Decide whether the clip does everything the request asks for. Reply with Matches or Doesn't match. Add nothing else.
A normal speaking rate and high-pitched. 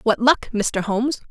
Matches